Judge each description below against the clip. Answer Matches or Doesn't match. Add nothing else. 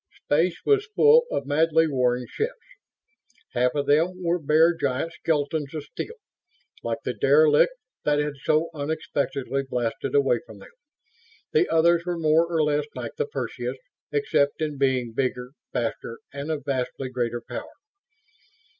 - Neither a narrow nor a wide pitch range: Matches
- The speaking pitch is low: Doesn't match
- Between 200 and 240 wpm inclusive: Doesn't match